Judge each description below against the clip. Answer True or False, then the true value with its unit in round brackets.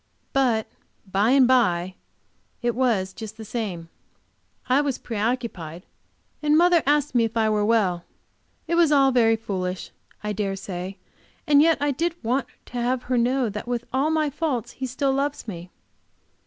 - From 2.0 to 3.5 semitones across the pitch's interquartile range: False (4.8 semitones)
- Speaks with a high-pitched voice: True (240 Hz)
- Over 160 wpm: True (170 wpm)